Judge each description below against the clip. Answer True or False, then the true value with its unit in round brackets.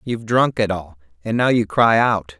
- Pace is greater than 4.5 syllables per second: True (4.9 syllables/s)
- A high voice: False (105 Hz)